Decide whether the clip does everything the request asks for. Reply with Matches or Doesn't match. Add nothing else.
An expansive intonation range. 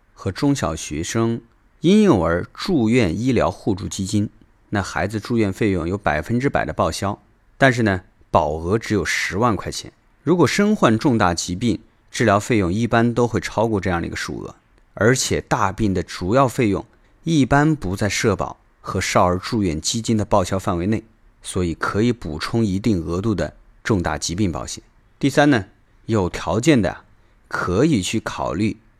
Doesn't match